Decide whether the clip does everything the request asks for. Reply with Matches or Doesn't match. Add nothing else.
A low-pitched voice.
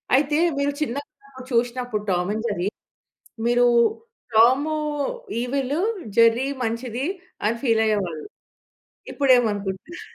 Doesn't match